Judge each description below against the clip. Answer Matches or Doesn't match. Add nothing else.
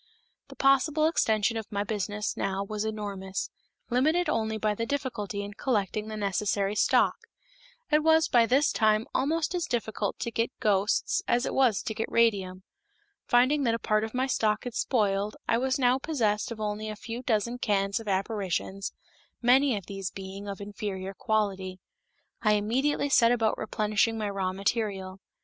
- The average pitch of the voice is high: Matches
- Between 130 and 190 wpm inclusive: Matches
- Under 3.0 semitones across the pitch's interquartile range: Doesn't match